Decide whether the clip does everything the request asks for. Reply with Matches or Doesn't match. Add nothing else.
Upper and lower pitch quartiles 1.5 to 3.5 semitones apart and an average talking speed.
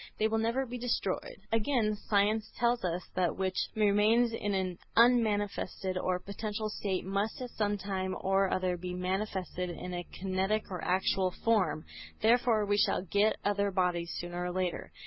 Matches